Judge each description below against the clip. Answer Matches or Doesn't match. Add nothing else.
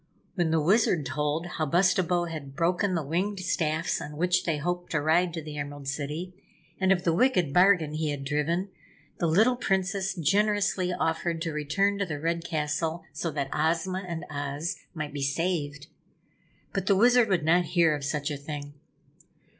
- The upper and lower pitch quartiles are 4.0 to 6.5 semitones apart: Doesn't match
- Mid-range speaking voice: Matches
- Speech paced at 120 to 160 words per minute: Doesn't match